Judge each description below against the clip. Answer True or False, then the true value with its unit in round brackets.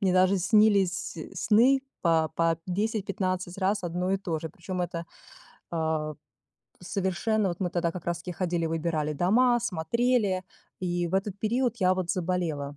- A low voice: False (185 Hz)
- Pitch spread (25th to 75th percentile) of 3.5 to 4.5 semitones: False (3.1 semitones)